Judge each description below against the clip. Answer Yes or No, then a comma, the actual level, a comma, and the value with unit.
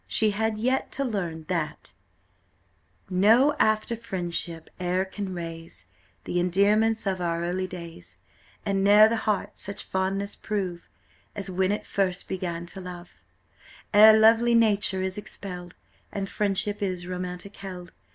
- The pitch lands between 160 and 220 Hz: Yes, high, 190 Hz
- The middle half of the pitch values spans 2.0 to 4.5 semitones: Yes, average, 2.9 semitones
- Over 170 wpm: No, average, 140 wpm